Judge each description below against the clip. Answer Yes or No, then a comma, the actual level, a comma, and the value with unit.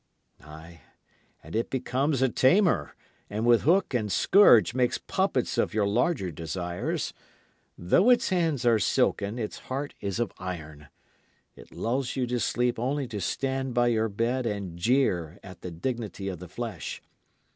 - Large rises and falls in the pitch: Yes, wide, 5.9 semitones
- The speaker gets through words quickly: No, average, 155 wpm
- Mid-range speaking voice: No, low, 115 Hz